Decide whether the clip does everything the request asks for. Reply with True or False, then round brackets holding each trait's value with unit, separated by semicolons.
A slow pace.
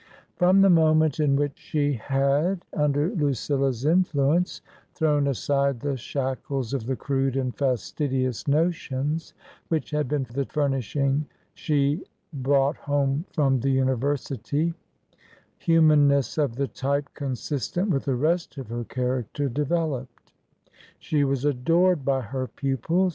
True (130 wpm)